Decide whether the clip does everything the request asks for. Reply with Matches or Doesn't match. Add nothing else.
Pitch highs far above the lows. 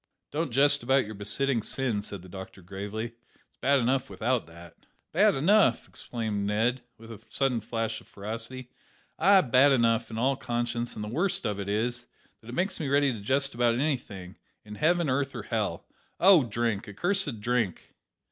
Doesn't match